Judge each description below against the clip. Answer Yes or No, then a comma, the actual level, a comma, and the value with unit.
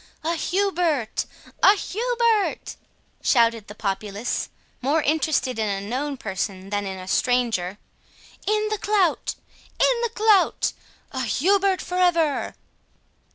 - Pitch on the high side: Yes, very high, 295 Hz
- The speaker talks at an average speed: No, slow, 110 wpm